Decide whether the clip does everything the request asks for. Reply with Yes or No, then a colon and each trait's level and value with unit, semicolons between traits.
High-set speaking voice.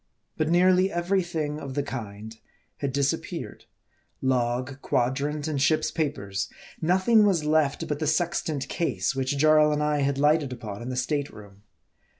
No: medium, 145 Hz